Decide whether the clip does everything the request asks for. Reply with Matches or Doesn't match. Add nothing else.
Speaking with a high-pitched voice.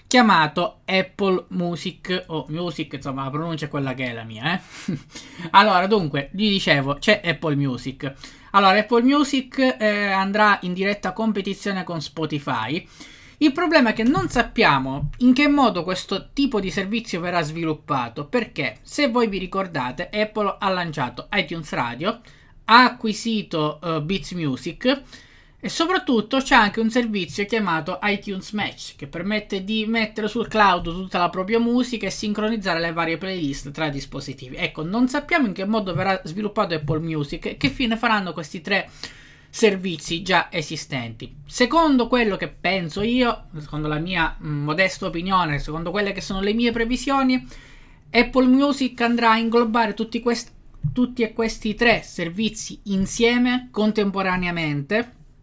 Matches